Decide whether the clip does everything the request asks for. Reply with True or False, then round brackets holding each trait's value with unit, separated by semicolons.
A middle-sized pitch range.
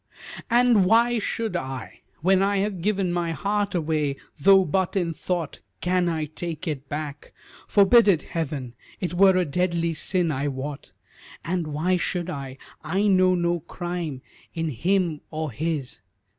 True (3.8 semitones)